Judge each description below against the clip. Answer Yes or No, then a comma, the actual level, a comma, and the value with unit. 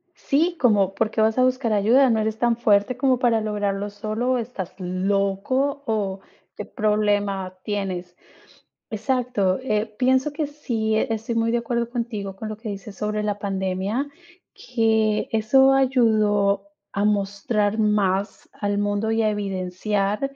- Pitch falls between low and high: No, high, 215 Hz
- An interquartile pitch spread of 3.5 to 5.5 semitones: No, average, 2.9 semitones